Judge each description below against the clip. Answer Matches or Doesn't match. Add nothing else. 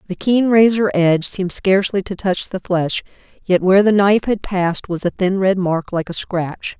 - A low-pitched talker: Doesn't match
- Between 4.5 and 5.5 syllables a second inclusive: Matches